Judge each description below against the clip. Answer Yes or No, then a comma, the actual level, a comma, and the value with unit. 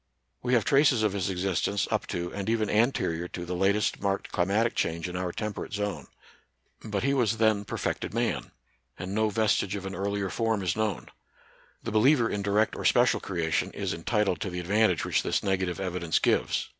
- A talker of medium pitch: No, low, 100 Hz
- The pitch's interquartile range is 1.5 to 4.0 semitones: Yes, average, 3.2 semitones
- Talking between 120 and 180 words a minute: No, average, 195 wpm